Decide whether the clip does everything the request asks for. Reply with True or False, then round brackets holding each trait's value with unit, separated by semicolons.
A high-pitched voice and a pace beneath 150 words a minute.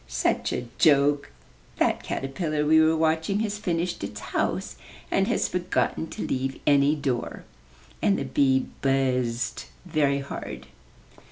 False (140 Hz; 135 wpm)